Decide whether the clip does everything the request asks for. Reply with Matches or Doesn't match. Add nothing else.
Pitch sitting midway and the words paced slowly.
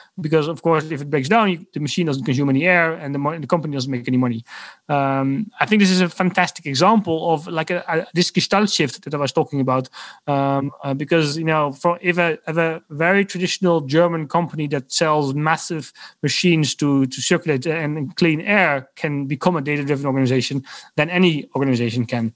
Doesn't match